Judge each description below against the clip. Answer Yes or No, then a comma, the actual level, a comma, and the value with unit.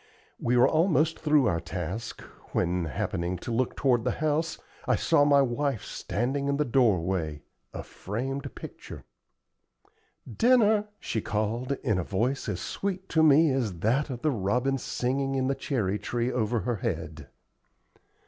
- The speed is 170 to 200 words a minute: No, average, 155 wpm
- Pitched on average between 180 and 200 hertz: No, low, 125 Hz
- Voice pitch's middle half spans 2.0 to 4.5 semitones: No, wide, 5.5 semitones